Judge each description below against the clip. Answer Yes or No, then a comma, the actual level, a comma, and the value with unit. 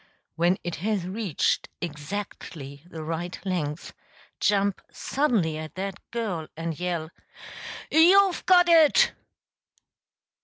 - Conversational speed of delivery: No, slow, 105 wpm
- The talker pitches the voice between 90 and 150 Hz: No, medium, 180 Hz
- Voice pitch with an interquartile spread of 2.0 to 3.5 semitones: No, average, 5.3 semitones